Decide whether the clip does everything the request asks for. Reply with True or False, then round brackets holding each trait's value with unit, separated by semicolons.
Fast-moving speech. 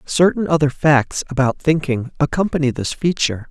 False (135 wpm)